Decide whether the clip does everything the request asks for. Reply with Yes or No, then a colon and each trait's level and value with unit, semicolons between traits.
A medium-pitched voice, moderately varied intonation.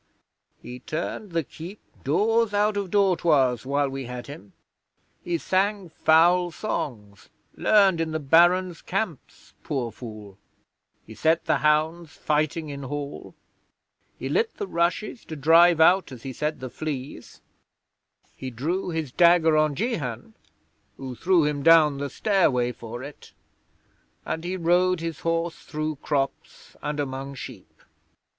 Yes: medium, 155 Hz; average, 4.4 semitones